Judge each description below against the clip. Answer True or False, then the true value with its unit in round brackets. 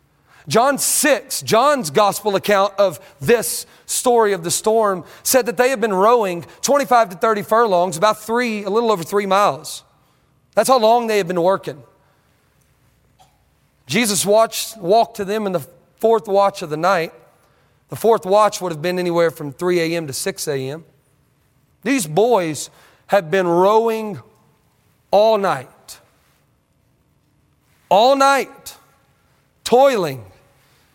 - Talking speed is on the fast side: False (135 wpm)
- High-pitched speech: True (200 Hz)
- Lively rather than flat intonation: False (4.4 semitones)